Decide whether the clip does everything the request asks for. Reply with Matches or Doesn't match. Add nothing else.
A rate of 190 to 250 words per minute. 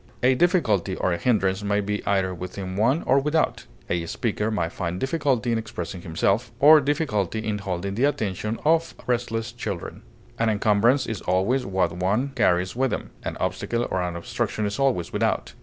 Doesn't match